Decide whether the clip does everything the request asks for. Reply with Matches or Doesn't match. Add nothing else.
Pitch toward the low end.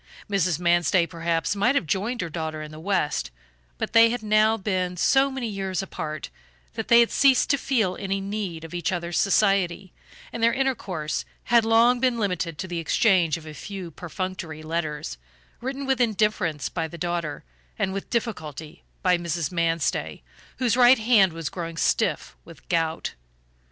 Doesn't match